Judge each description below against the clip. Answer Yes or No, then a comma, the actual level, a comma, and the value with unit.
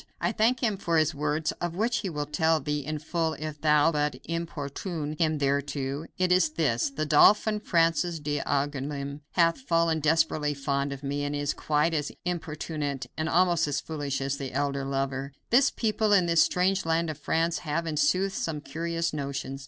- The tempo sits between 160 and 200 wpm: Yes, average, 185 wpm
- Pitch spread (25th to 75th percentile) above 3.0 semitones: No, average, 2.7 semitones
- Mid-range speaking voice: Yes, medium, 155 Hz